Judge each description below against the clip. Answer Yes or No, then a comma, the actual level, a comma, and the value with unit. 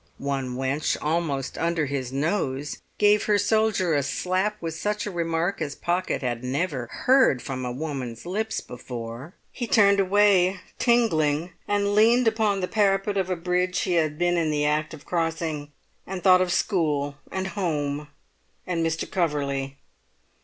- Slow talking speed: No, average, 160 wpm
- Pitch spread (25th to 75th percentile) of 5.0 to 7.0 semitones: Yes, wide, 5.4 semitones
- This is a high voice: No, medium, 170 Hz